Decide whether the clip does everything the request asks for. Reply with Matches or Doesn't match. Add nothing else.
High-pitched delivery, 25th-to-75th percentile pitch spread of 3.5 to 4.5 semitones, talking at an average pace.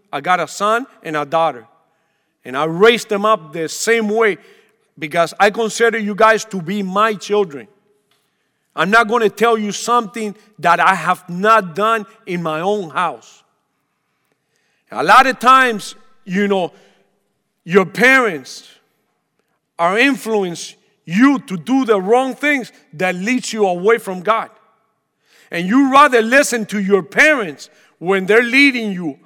Matches